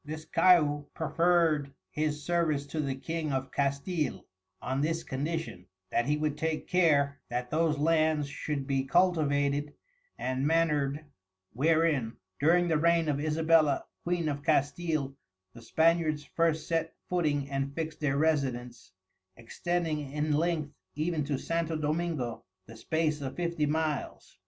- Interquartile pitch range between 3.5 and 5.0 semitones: No, average, 2.7 semitones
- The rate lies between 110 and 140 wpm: Yes, slow, 135 wpm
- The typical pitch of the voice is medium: Yes, medium, 150 Hz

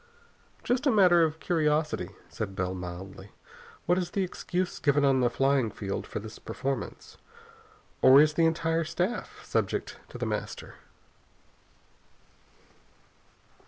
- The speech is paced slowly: Yes, slow, 130 wpm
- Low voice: No, medium, 150 Hz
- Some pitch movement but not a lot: No, wide, 7.3 semitones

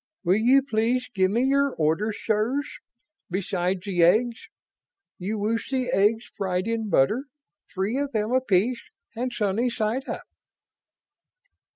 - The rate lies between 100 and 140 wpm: Yes, slow, 135 wpm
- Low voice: No, high, 220 Hz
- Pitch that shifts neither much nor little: Yes, average, 4.4 semitones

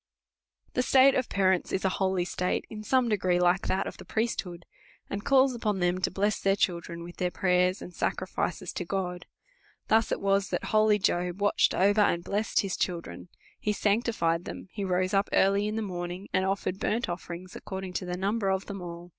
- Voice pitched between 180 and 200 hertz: Yes, high, 190 Hz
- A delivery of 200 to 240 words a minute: Yes, fast, 205 wpm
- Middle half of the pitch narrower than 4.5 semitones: Yes, average, 2.7 semitones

